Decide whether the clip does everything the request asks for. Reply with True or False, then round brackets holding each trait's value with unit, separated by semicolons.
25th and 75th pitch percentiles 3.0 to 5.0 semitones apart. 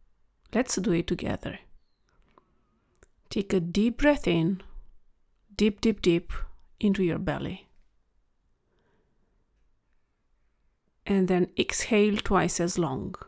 True (3.5 semitones)